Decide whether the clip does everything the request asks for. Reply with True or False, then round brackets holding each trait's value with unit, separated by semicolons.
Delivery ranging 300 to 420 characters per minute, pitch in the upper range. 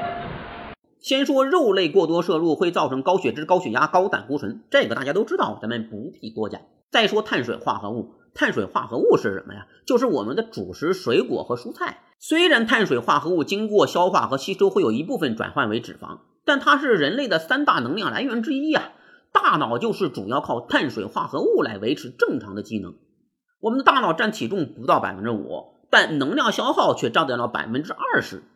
True (315 characters per minute; 270 Hz)